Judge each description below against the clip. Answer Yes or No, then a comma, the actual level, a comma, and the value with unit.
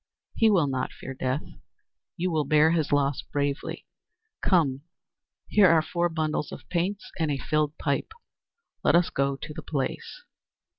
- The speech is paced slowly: No, average, 155 wpm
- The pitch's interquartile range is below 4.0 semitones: Yes, average, 3.4 semitones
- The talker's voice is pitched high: No, medium, 155 Hz